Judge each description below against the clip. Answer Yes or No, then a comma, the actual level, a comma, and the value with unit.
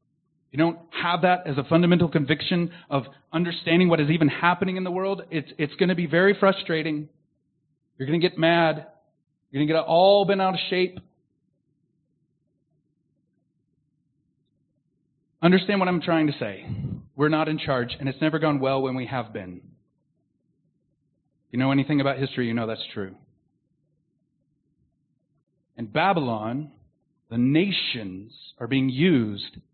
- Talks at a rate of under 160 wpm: Yes, average, 145 wpm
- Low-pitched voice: No, medium, 155 Hz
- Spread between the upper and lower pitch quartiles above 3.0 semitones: No, average, 2.7 semitones